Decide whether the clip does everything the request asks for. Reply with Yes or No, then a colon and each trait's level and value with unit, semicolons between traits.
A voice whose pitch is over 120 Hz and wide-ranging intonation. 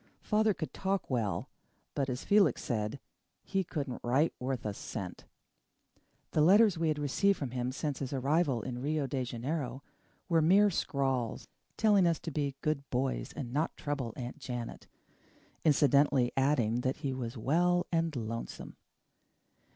No: medium, 140 Hz; average, 4.6 semitones